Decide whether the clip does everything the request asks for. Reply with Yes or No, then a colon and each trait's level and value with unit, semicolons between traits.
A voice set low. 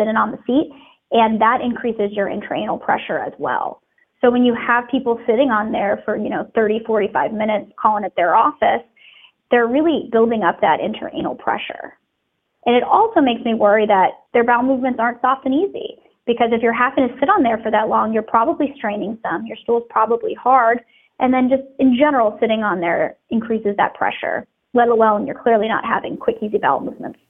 No: high, 240 Hz